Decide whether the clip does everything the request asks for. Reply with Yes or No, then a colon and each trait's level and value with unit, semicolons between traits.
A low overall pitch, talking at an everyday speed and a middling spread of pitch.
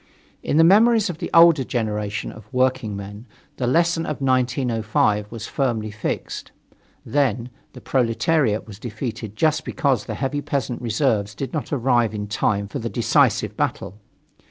Yes: low, 120 Hz; average, 150 wpm; average, 4.6 semitones